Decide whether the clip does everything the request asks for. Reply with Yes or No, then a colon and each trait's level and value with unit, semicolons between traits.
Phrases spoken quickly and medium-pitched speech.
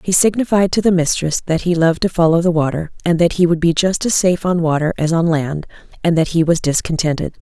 Yes: fast, 240 wpm; medium, 170 Hz